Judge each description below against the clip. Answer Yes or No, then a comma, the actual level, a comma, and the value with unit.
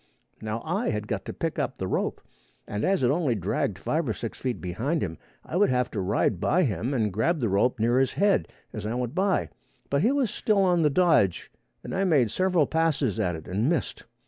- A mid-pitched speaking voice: No, low, 130 Hz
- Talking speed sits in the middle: No, fast, 225 wpm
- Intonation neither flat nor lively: No, wide, 8.2 semitones